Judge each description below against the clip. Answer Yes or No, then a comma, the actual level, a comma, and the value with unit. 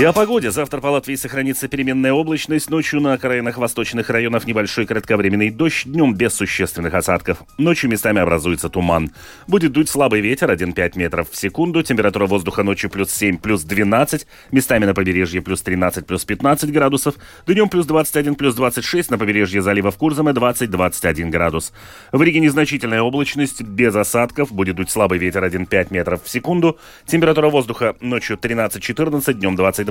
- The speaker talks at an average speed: No, fast, 165 wpm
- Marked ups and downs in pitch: Yes, wide, 7.0 semitones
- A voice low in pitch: Yes, low, 115 Hz